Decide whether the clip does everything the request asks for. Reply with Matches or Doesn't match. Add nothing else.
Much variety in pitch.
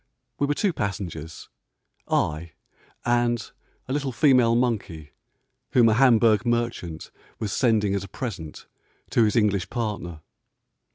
Doesn't match